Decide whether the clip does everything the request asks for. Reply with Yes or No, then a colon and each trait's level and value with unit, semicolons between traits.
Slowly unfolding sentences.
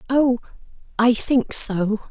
Yes: slow, 115 wpm